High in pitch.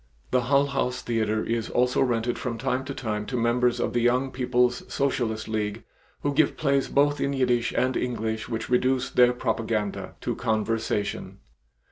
No: low, 120 Hz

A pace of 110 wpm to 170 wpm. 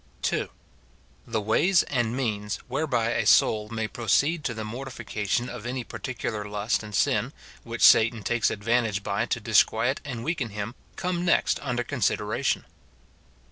Yes: average, 145 wpm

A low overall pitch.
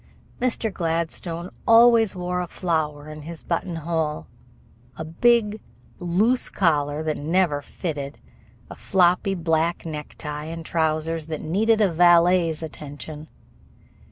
No: medium, 165 Hz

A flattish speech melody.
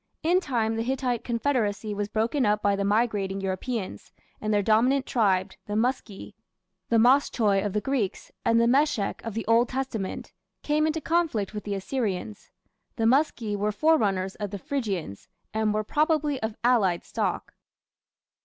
No: average, 4.1 semitones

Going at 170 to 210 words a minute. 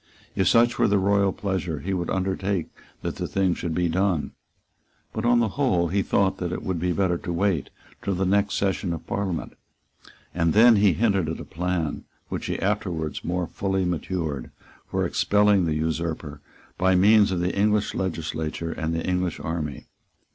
Yes: average, 180 wpm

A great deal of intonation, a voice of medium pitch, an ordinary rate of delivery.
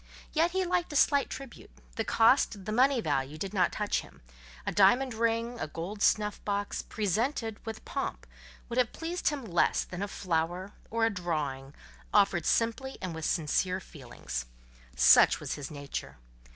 No: wide, 6.1 semitones; high, 205 Hz; average, 165 wpm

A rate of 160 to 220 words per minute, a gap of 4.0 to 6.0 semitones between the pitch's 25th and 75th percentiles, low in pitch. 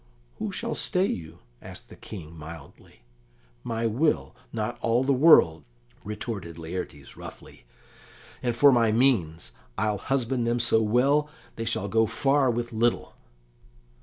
No: slow, 135 wpm; average, 5.2 semitones; low, 115 Hz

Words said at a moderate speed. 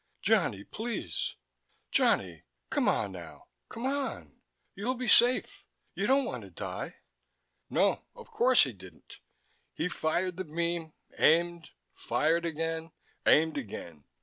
No: slow, 125 wpm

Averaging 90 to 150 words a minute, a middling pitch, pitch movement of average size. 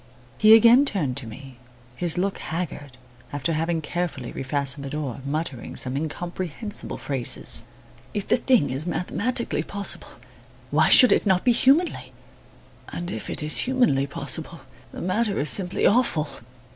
No: average, 145 wpm; medium, 170 Hz; wide, 6.6 semitones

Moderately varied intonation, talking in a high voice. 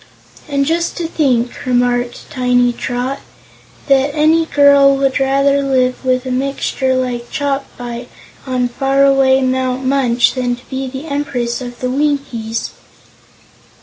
No: narrow, 2.0 semitones; very high, 265 Hz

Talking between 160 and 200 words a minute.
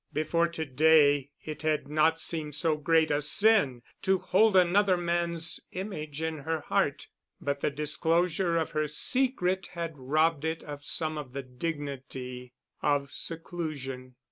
No: average, 145 wpm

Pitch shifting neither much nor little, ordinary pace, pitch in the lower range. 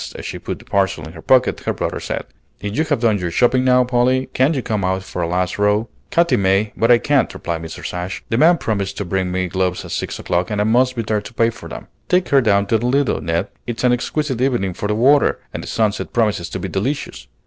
No: average, 4.9 semitones; fast, 260 wpm; low, 110 Hz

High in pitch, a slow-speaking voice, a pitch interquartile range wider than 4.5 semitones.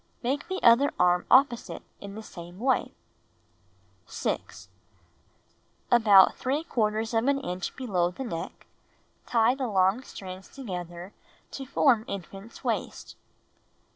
Yes: high, 220 Hz; slow, 115 wpm; wide, 5.6 semitones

